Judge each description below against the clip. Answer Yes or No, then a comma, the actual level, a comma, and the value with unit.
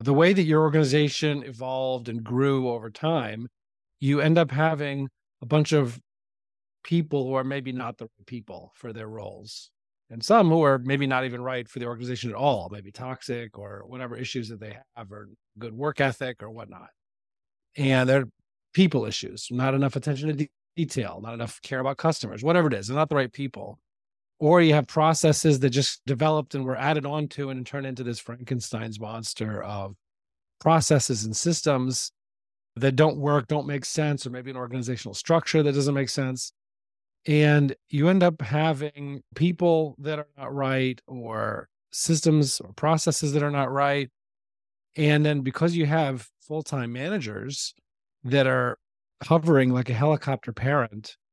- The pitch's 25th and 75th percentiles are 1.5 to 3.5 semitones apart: No, average, 4.0 semitones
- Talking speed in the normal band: Yes, average, 170 wpm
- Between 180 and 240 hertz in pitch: No, low, 135 Hz